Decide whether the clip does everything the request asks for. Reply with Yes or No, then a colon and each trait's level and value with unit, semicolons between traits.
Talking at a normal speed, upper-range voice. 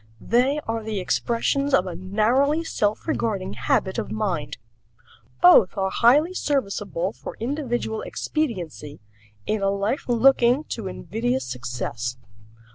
No: slow, 120 wpm; high, 220 Hz